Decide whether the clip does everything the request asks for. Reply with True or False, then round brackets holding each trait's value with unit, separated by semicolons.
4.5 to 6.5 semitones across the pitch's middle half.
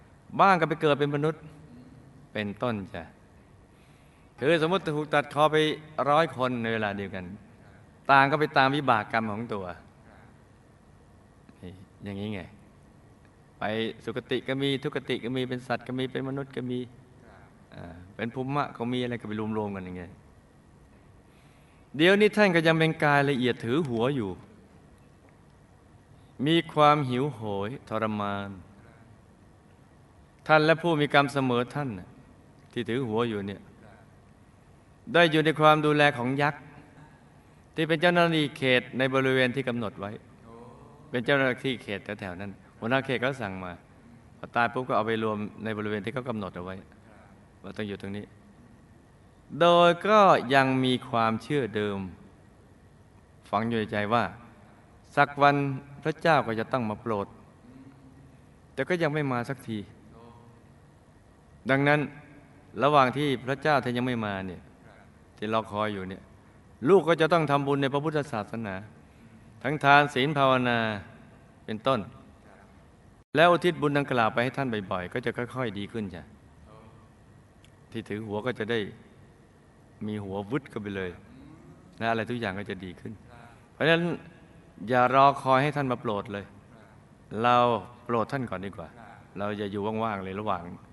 True (5.1 semitones)